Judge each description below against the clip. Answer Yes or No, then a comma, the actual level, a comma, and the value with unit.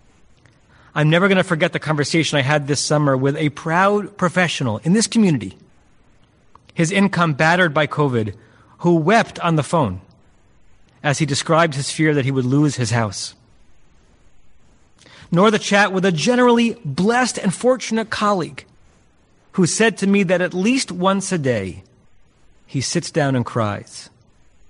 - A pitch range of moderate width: No, wide, 7.1 semitones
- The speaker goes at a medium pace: Yes, average, 155 wpm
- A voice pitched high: No, medium, 155 Hz